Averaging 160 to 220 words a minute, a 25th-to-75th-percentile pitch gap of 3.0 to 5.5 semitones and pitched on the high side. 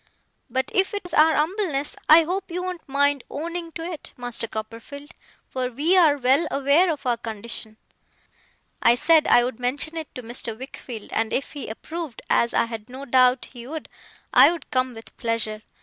Yes: average, 185 wpm; average, 5.2 semitones; very high, 275 Hz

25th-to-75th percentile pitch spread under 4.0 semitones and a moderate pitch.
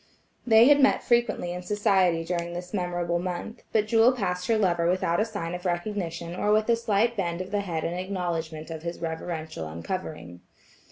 Yes: average, 3.6 semitones; medium, 180 Hz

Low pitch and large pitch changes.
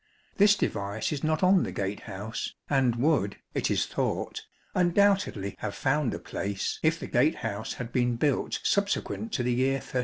Yes: low, 130 Hz; wide, 6.6 semitones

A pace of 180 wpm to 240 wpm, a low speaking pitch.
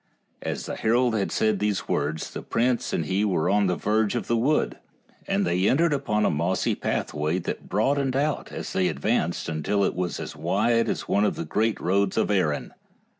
Yes: average, 200 wpm; low, 100 Hz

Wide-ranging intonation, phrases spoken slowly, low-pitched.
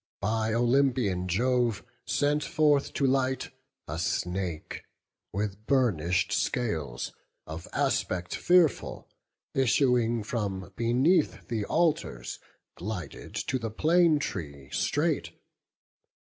Yes: wide, 6.6 semitones; slow, 95 wpm; low, 115 Hz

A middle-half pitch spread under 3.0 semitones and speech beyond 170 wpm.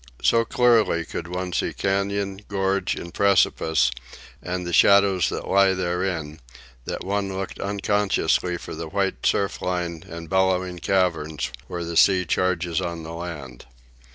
No: narrow, 2.5 semitones; average, 145 wpm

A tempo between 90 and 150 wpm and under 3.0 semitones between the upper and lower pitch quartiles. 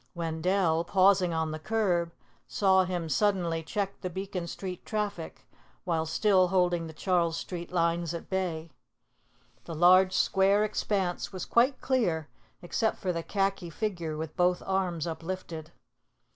Yes: average, 140 wpm; narrow, 2.5 semitones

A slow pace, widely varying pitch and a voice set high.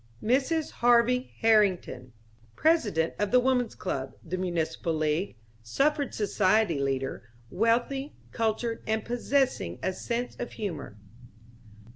Yes: slow, 110 wpm; wide, 6.9 semitones; high, 220 Hz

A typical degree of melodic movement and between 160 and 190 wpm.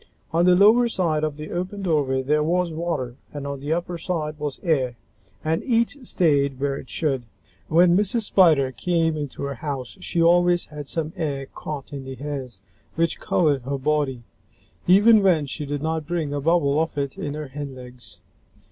Yes: average, 3.7 semitones; average, 185 wpm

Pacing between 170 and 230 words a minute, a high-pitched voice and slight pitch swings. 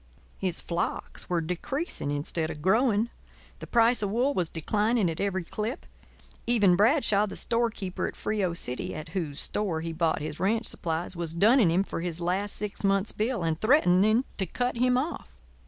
No: average, 175 wpm; high, 195 Hz; average, 5.1 semitones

